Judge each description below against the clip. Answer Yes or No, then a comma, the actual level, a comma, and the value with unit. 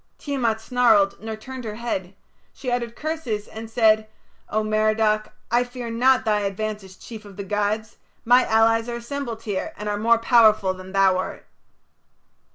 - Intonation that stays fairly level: Yes, narrow, 2.2 semitones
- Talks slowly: No, average, 165 wpm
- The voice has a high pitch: Yes, high, 220 Hz